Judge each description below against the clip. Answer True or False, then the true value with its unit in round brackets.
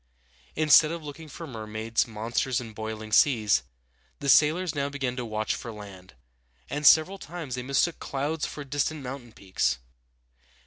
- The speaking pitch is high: False (130 Hz)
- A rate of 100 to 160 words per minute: True (150 wpm)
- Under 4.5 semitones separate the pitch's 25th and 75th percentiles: False (5.4 semitones)